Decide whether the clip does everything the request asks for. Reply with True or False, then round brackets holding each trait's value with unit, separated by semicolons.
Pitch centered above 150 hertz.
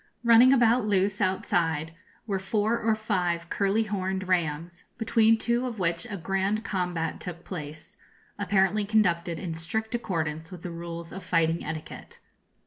True (190 Hz)